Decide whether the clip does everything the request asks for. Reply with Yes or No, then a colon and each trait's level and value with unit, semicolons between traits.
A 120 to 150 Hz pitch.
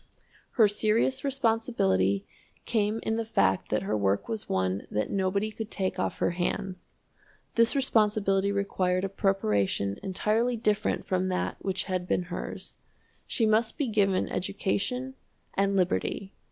No: high, 195 Hz